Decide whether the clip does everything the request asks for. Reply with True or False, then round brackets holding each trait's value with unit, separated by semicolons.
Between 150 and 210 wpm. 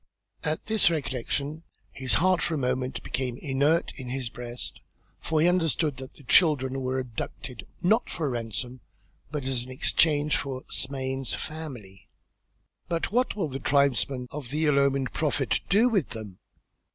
True (160 wpm)